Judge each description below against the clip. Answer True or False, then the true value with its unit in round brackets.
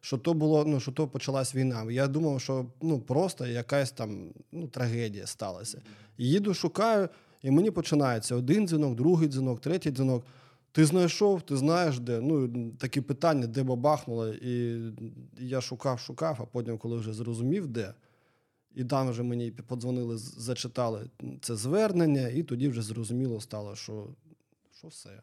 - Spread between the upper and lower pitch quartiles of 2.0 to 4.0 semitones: False (4.5 semitones)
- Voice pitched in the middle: False (130 Hz)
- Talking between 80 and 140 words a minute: False (155 wpm)